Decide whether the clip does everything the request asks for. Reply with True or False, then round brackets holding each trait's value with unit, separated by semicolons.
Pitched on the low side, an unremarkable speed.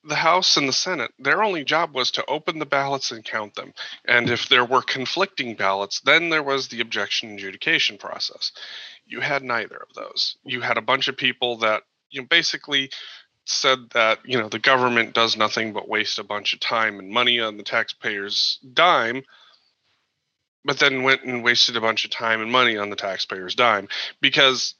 True (120 Hz; 195 wpm)